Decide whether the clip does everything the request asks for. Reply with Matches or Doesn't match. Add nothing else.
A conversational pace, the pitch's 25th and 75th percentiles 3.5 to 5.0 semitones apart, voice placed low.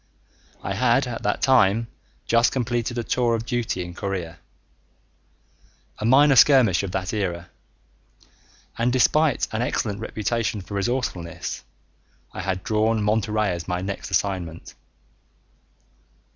Doesn't match